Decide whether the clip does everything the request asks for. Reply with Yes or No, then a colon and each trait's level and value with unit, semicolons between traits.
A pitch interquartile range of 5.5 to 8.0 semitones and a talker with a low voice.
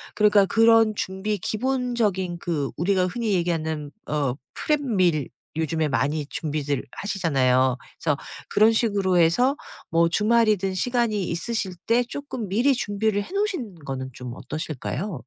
No: wide, 6.2 semitones; high, 190 Hz